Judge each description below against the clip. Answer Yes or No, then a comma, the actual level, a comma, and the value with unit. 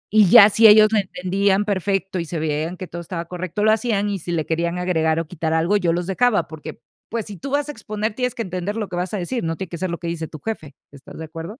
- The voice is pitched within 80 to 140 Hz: No, medium, 185 Hz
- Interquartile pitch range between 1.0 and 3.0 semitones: No, average, 3.9 semitones